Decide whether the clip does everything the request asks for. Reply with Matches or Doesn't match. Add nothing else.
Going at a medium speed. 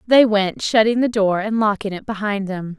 Doesn't match